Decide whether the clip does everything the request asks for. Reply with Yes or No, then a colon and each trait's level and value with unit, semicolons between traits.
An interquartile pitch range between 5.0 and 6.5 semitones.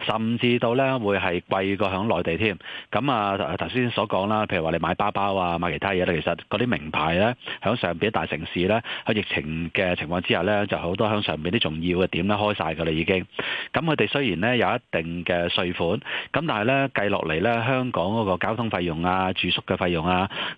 No: average, 4.4 semitones